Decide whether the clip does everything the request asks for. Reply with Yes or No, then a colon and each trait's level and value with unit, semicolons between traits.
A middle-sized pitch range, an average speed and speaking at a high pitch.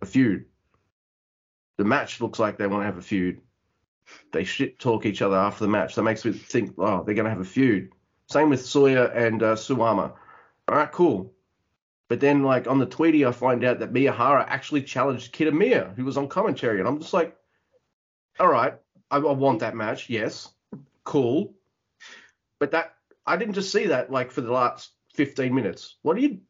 No: average, 4.6 semitones; average, 195 wpm; low, 125 Hz